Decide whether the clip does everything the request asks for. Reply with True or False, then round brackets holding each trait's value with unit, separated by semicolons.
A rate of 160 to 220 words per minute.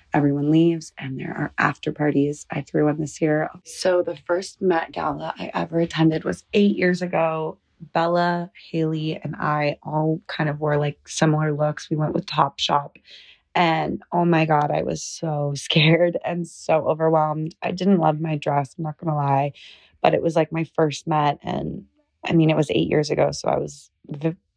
True (190 wpm)